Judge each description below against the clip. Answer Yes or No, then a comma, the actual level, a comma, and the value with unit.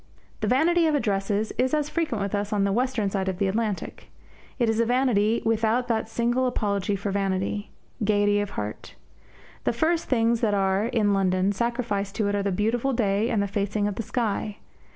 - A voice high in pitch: Yes, high, 210 Hz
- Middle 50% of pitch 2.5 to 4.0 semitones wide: Yes, average, 3.0 semitones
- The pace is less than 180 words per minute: No, average, 200 wpm